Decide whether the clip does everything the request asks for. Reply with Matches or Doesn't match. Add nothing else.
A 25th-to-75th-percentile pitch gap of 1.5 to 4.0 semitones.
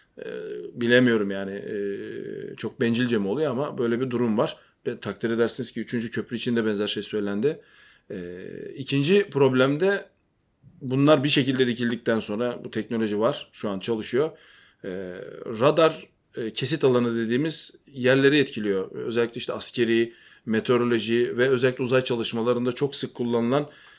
Matches